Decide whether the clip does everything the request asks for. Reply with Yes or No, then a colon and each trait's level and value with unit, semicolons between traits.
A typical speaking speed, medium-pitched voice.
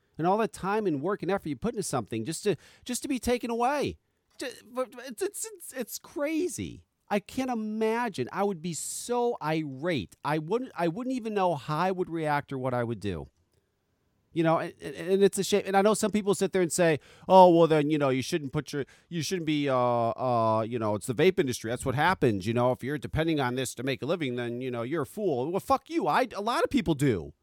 No: fast, 245 wpm; medium, 165 Hz